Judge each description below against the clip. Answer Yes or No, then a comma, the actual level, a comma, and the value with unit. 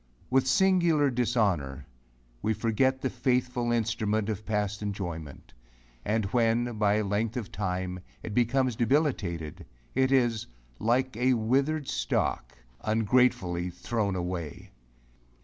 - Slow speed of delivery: Yes, slow, 115 wpm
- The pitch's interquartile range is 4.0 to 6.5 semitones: Yes, average, 4.4 semitones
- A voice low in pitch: Yes, low, 110 Hz